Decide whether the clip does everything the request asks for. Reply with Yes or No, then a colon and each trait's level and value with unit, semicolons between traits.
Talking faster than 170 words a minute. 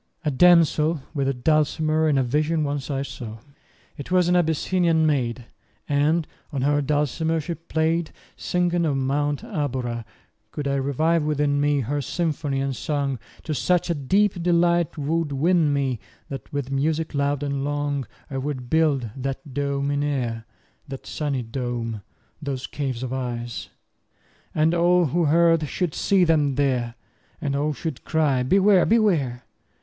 No: average, 160 wpm